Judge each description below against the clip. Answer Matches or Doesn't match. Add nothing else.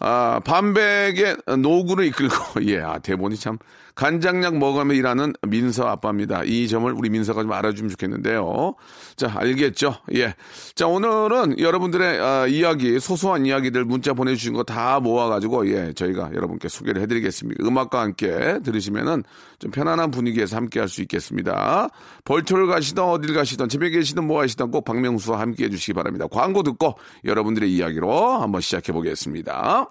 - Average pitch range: Doesn't match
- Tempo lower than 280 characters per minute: Doesn't match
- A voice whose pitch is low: Matches